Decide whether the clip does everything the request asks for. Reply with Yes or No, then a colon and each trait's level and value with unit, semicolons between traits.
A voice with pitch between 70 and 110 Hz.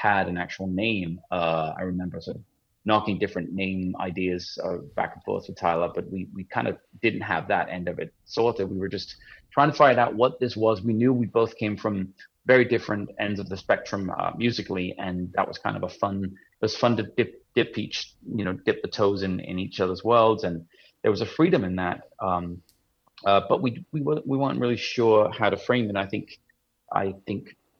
Yes: low, 100 Hz